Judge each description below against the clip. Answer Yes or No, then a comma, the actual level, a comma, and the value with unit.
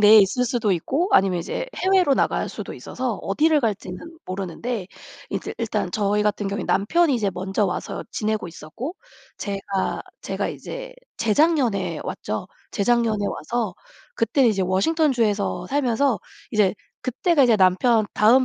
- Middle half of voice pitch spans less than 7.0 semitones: Yes, wide, 5.4 semitones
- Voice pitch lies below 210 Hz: No, high, 220 Hz